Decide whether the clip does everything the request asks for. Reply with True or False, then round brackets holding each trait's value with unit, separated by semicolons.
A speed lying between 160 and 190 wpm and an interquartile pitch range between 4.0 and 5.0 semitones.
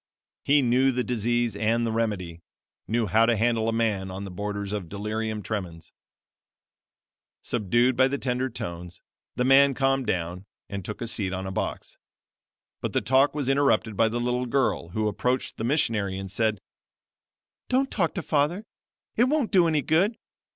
True (175 wpm; 4.6 semitones)